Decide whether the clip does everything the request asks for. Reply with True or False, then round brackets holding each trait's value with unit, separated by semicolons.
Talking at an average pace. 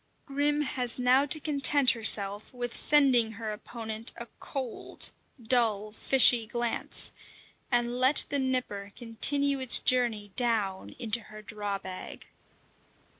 False (125 wpm)